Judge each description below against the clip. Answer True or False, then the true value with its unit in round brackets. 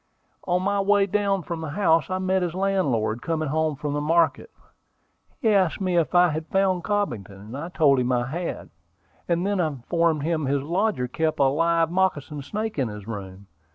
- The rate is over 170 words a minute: True (190 wpm)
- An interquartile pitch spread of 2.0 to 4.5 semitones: False (5.0 semitones)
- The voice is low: False (165 Hz)